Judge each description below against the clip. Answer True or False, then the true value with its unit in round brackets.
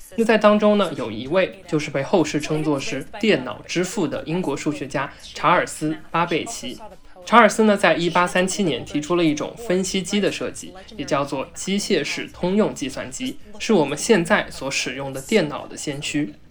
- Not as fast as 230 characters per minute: False (270 characters per minute)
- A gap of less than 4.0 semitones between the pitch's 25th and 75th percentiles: False (5.3 semitones)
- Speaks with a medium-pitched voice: True (175 Hz)